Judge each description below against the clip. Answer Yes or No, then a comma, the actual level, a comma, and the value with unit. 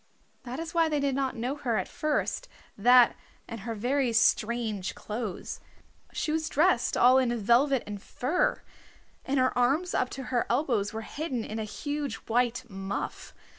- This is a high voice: Yes, high, 245 Hz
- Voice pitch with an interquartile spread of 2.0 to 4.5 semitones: Yes, average, 3.8 semitones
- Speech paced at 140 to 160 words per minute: No, average, 170 wpm